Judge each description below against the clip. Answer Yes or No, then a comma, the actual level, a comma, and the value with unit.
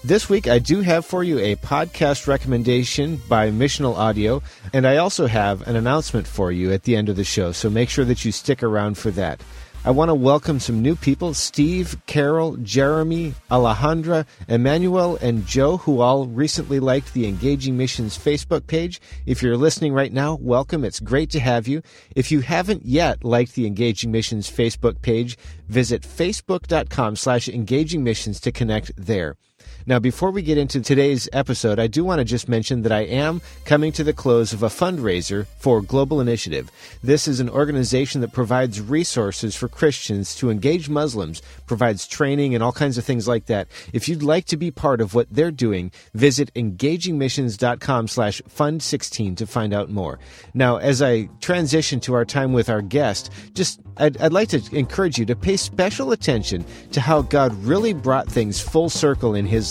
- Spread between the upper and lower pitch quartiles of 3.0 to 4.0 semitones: No, average, 4.9 semitones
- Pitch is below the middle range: Yes, low, 125 Hz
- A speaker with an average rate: Yes, average, 185 wpm